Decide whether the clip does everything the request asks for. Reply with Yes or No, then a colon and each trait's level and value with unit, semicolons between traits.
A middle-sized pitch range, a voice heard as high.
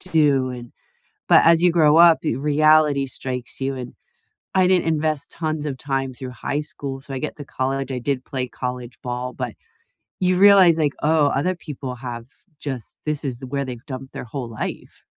No: average, 3.3 semitones; medium, 140 Hz